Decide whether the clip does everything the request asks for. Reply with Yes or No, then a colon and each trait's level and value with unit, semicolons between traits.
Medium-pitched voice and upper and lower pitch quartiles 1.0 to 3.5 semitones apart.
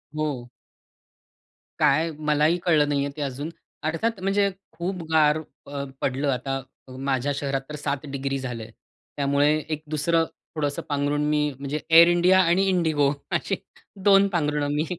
Yes: medium, 150 Hz; average, 2.8 semitones